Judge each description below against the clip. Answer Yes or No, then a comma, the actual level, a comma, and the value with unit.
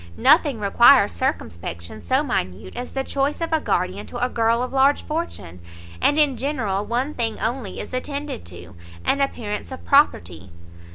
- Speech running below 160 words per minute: No, average, 165 wpm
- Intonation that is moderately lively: No, wide, 6.8 semitones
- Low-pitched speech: No, high, 245 Hz